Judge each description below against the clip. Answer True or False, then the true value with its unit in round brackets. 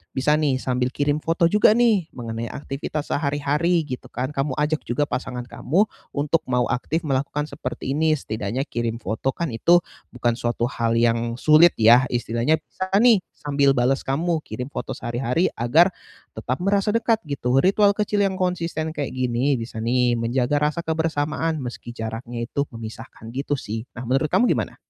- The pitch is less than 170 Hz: True (140 Hz)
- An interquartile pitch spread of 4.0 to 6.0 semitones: True (4.7 semitones)